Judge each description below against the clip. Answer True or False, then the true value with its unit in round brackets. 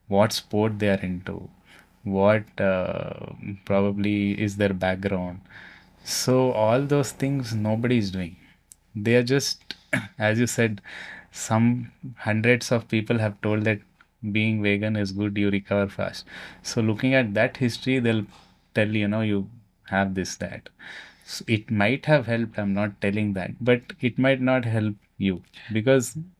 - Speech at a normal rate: True (150 wpm)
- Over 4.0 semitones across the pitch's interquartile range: False (3.1 semitones)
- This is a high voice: False (110 Hz)